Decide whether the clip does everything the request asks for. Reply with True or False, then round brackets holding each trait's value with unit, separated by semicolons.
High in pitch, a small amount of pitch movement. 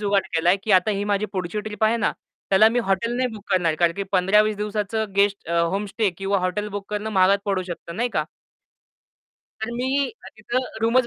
True (205 Hz; 2.3 semitones)